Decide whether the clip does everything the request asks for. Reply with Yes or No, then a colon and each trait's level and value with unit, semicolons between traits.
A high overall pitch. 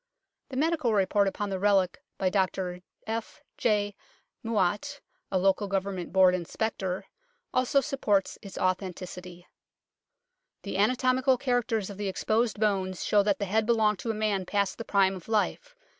Yes: high, 205 Hz